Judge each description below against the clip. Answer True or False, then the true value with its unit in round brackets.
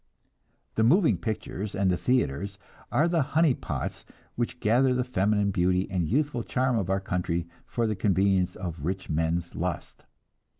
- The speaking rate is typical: True (160 wpm)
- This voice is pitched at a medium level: False (100 Hz)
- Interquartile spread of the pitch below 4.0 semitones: False (5.5 semitones)